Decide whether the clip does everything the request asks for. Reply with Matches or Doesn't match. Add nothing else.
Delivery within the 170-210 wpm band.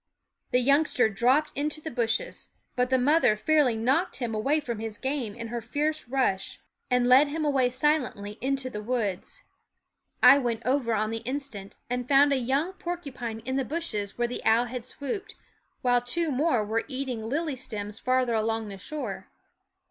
Matches